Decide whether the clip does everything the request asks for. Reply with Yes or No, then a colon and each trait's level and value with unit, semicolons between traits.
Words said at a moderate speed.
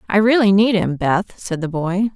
No: fast, 220 wpm